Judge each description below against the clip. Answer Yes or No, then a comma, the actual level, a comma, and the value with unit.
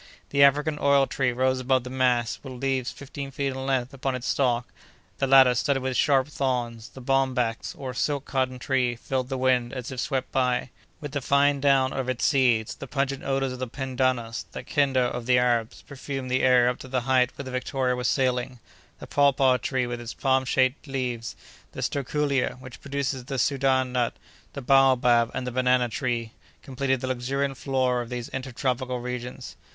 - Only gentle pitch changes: Yes, narrow, 1.5 semitones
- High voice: No, low, 130 Hz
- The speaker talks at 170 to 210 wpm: Yes, average, 195 wpm